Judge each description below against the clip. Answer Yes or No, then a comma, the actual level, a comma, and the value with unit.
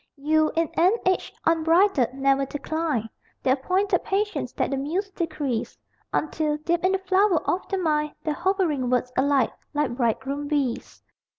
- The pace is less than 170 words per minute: Yes, average, 155 wpm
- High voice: Yes, very high, 310 Hz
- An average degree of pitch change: Yes, average, 5.0 semitones